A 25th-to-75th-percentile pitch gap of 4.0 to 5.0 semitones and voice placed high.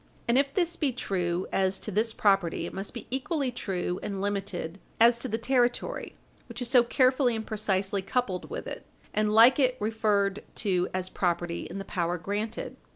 Yes: average, 4.4 semitones; high, 210 Hz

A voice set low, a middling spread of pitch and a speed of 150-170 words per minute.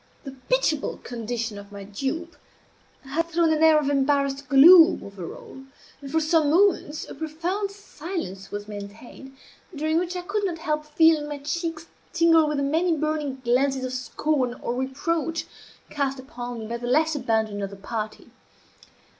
No: very high, 290 Hz; average, 4.7 semitones; average, 165 wpm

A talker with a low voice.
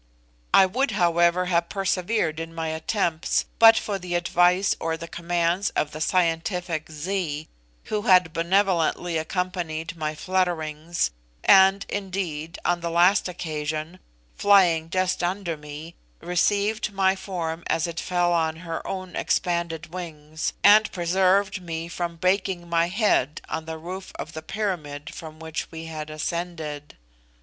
No: medium, 170 Hz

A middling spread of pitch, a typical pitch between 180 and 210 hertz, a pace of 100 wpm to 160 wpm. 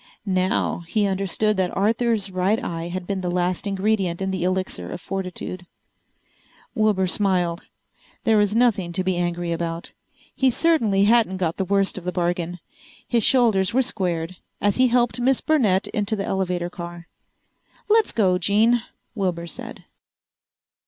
Yes: average, 3.4 semitones; high, 190 Hz; average, 150 wpm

